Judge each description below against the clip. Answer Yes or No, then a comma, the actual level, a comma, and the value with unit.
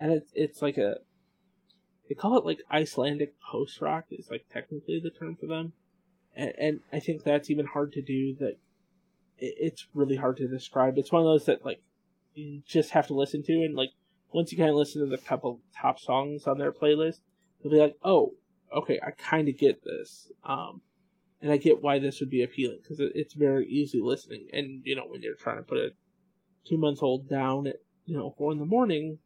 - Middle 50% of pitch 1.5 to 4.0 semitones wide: No, average, 4.7 semitones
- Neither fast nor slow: No, fast, 215 wpm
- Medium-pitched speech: Yes, medium, 150 Hz